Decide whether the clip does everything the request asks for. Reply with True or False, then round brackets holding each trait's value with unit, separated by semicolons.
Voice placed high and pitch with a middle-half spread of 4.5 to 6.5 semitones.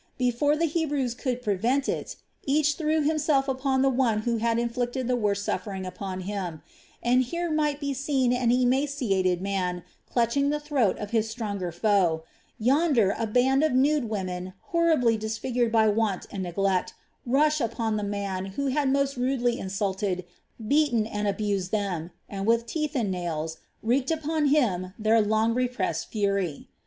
True (235 Hz; 5.4 semitones)